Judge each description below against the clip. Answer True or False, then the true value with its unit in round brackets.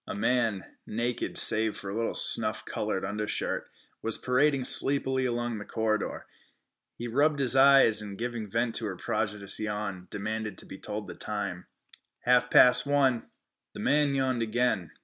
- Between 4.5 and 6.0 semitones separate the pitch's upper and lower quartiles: False (3.2 semitones)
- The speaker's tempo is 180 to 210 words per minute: False (160 wpm)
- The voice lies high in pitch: False (115 Hz)